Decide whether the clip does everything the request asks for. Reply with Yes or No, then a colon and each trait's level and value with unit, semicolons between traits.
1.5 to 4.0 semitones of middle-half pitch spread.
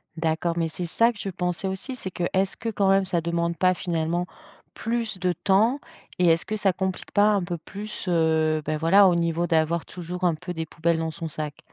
Yes: average, 2.8 semitones